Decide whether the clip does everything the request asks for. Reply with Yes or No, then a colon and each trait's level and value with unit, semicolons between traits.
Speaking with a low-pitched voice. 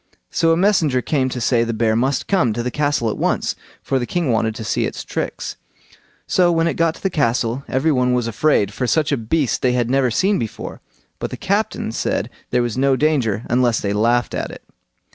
Yes: low, 125 Hz